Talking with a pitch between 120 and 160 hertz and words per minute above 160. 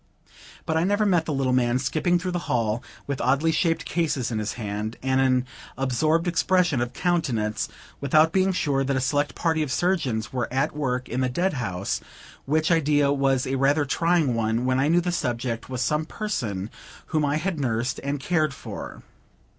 Yes: medium, 140 Hz; average, 190 wpm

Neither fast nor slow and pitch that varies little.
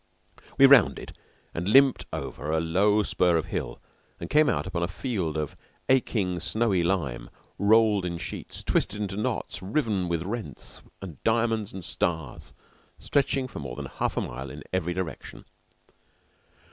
No: average, 155 wpm; average, 5.1 semitones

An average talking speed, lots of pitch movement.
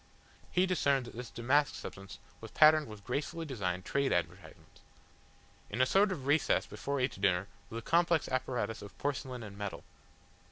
Yes: average, 165 wpm; wide, 6.2 semitones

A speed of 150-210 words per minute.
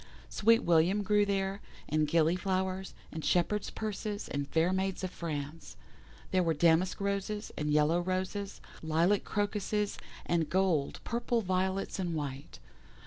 No: average, 140 wpm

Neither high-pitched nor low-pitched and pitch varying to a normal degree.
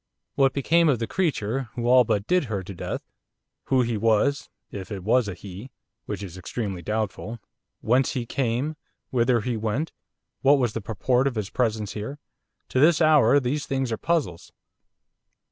No: low, 120 Hz; average, 4.3 semitones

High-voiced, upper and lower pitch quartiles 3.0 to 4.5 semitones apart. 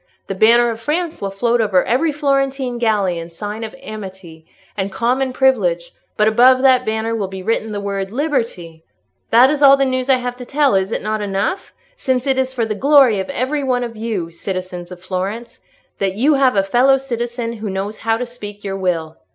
No: high, 225 Hz; average, 5.0 semitones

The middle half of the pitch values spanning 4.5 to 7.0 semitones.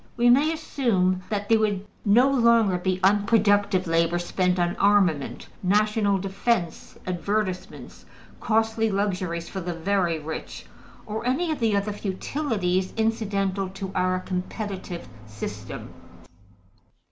No: average, 3.2 semitones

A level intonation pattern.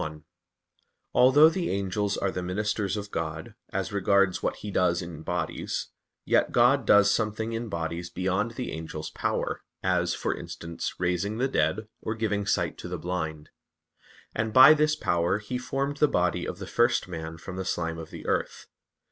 No: average, 4.6 semitones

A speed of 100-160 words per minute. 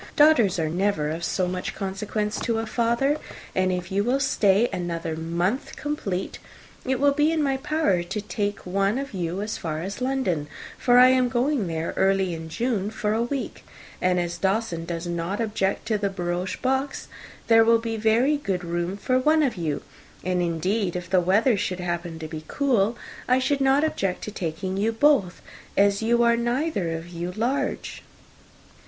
No: average, 185 wpm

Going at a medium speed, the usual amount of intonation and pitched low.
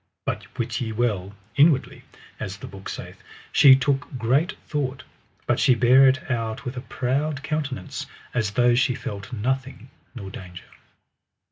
Yes: average, 150 wpm; average, 3.2 semitones; low, 125 Hz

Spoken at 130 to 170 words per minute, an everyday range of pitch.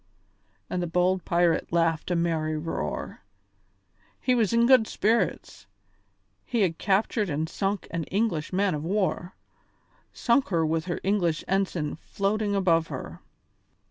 Yes: average, 140 wpm; average, 3.7 semitones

